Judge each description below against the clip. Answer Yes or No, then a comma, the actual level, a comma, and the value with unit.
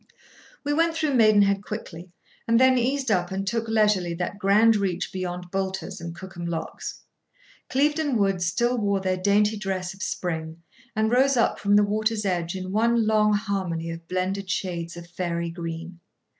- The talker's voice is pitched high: Yes, high, 195 Hz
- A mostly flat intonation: No, average, 3.7 semitones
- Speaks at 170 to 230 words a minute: Yes, average, 180 wpm